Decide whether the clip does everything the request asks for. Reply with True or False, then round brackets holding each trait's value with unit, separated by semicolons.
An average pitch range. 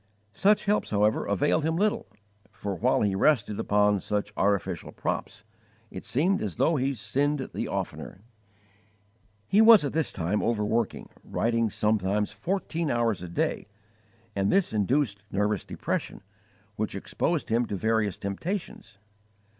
False (6.6 semitones)